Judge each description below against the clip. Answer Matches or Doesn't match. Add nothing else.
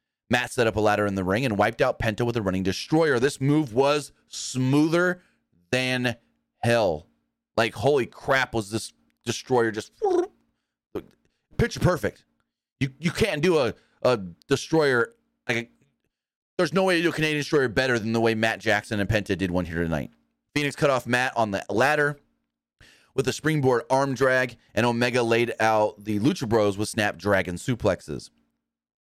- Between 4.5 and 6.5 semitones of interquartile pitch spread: Matches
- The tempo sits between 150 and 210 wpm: Matches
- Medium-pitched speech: Doesn't match